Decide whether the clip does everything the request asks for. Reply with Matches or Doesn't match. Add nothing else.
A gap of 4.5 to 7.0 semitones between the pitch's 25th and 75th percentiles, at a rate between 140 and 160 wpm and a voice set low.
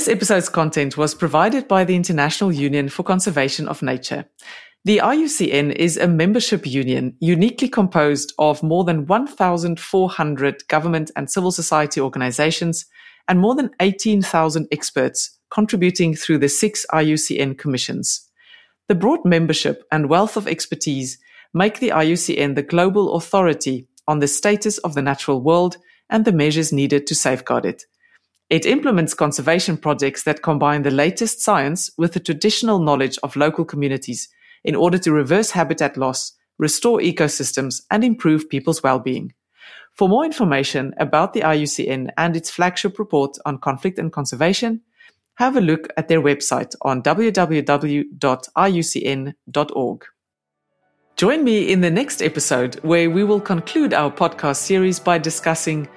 Doesn't match